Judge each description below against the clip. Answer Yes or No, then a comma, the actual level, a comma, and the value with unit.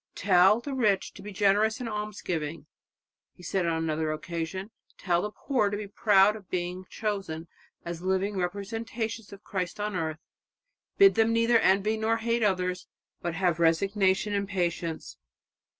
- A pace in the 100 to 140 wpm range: No, average, 160 wpm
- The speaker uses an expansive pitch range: No, average, 3.3 semitones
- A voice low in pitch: No, high, 195 Hz